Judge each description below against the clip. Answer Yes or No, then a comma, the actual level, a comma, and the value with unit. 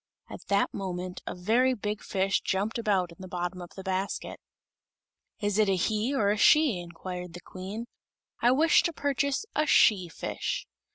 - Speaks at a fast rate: No, average, 175 wpm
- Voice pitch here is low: No, high, 200 Hz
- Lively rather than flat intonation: No, average, 4.2 semitones